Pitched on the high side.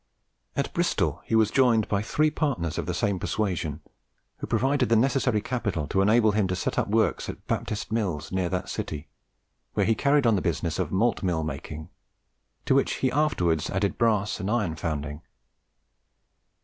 No: low, 105 Hz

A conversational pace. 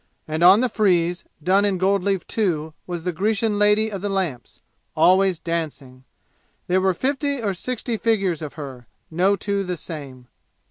Yes: average, 170 wpm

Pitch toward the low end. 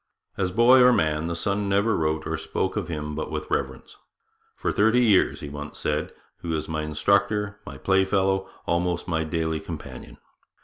Yes: very low, 85 Hz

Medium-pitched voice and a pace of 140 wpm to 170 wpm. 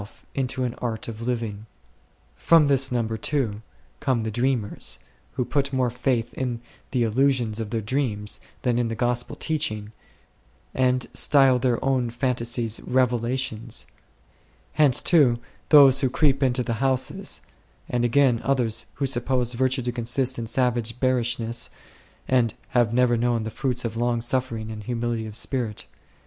No: low, 120 Hz; average, 150 wpm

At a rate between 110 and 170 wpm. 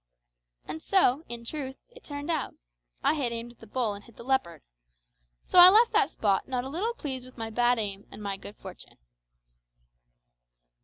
No: average, 190 wpm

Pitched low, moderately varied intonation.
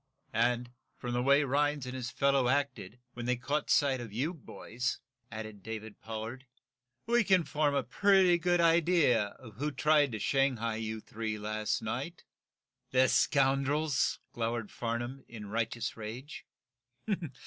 Yes: low, 125 Hz; average, 4.1 semitones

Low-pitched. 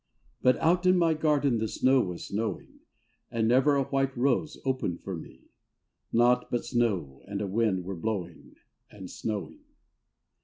Yes: low, 120 Hz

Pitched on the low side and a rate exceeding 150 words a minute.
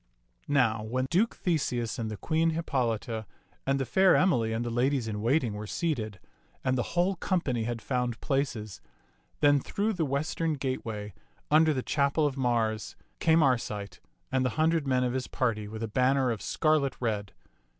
Yes: low, 130 Hz; average, 170 wpm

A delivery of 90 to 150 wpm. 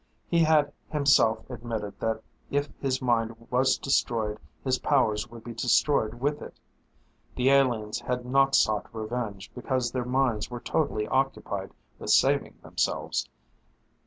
Yes: slow, 135 wpm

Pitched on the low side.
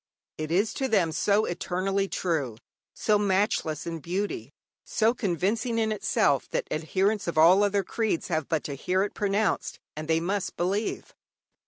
No: high, 190 Hz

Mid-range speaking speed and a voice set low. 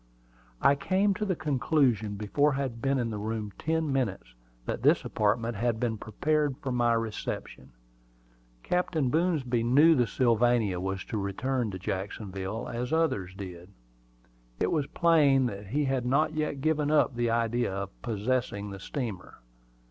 Yes: average, 160 wpm; low, 120 Hz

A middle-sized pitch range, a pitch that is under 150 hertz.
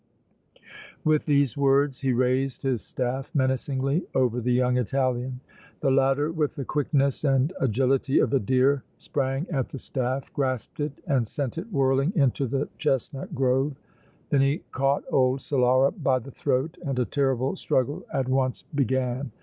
No: narrow, 1.5 semitones; low, 135 Hz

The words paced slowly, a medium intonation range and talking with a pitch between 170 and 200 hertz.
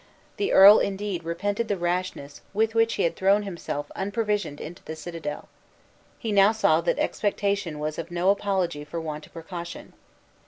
No: average, 160 wpm; average, 3.8 semitones; medium, 185 Hz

